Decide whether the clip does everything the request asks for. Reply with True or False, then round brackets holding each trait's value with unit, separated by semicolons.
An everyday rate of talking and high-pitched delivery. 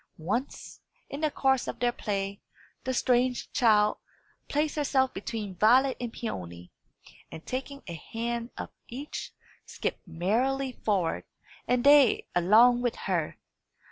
False (130 wpm; 240 Hz)